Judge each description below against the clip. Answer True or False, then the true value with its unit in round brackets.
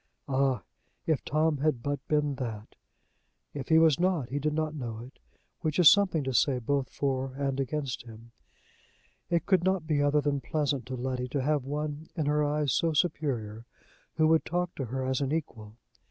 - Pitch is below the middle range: False (145 Hz)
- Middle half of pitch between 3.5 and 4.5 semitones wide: False (3.0 semitones)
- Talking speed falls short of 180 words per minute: False (190 wpm)